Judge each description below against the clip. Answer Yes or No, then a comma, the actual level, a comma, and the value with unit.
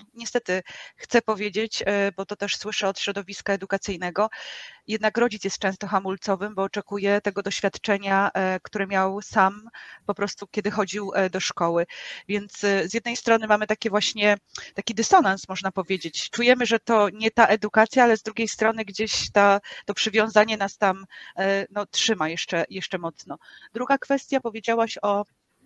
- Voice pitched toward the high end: Yes, high, 205 Hz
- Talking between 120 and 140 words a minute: No, average, 150 wpm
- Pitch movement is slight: Yes, narrow, 2.0 semitones